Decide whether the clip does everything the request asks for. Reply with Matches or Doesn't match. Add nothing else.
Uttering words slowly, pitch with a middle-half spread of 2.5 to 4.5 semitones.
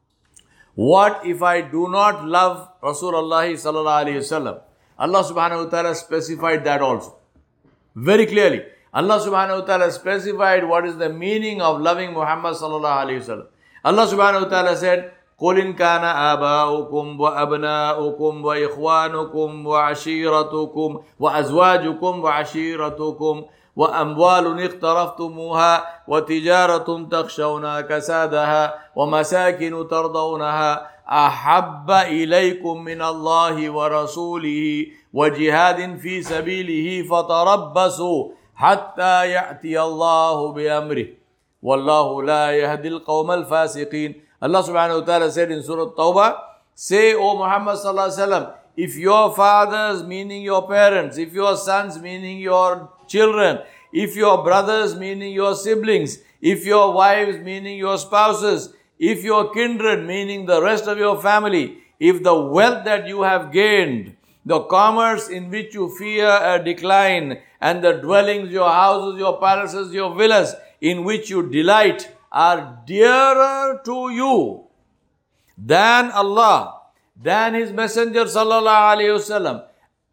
Matches